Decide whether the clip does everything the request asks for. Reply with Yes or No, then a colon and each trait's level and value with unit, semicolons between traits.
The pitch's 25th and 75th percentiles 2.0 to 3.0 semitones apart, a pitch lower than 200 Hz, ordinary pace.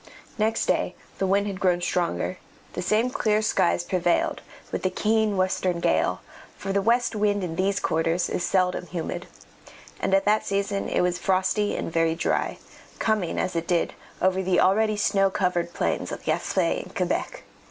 Yes: narrow, 2.5 semitones; high, 190 Hz; average, 175 wpm